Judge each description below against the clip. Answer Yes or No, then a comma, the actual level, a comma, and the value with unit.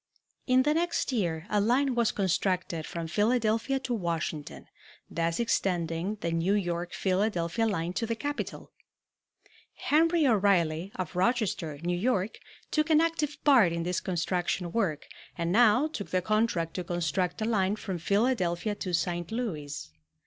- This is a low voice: No, high, 190 Hz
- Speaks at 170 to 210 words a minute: No, average, 150 wpm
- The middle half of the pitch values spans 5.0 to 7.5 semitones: Yes, average, 5.3 semitones